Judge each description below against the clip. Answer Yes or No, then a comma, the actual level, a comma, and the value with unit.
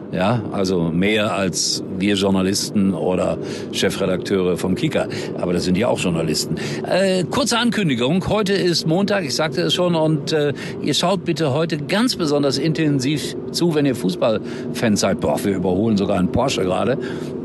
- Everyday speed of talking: Yes, average, 160 wpm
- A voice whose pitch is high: No, low, 135 Hz